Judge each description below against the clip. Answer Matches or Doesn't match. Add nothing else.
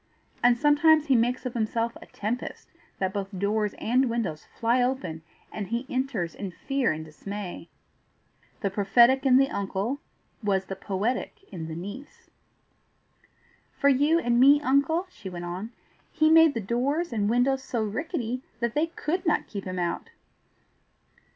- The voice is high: Matches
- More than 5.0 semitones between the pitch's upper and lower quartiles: Matches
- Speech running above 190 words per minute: Doesn't match